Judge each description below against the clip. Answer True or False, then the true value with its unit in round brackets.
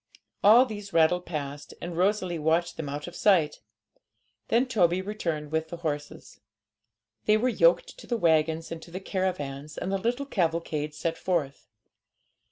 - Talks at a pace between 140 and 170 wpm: True (160 wpm)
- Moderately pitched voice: True (170 Hz)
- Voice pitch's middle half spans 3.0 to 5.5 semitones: True (4.2 semitones)